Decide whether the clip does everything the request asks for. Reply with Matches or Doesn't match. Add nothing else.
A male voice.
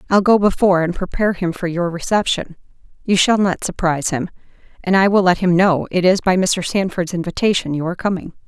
Doesn't match